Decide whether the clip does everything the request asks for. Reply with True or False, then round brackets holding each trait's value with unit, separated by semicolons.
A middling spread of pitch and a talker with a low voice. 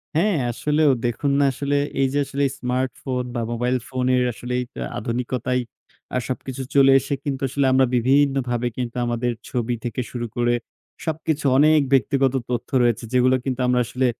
False (2.2 semitones; 130 Hz)